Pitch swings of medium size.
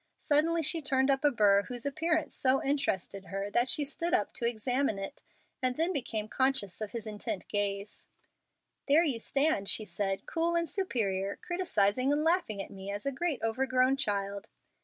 No: wide, 6.3 semitones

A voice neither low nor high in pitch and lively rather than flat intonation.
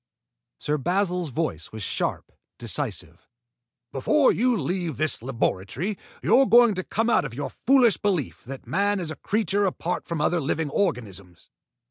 Yes: medium, 170 Hz; wide, 7.0 semitones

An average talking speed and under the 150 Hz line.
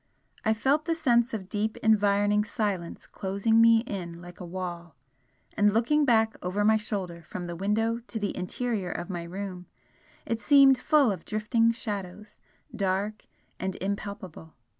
No: average, 155 wpm; high, 205 Hz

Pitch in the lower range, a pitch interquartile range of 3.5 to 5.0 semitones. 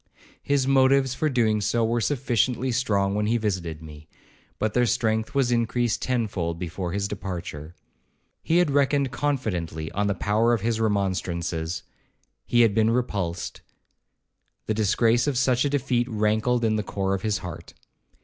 Yes: low, 110 Hz; average, 4.3 semitones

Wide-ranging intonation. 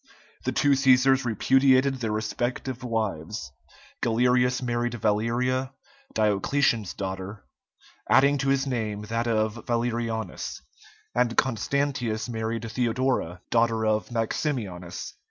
No: average, 2.9 semitones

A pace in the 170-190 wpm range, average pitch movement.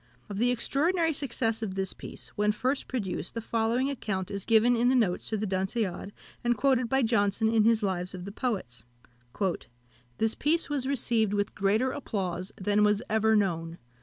Yes: average, 180 wpm; average, 3.8 semitones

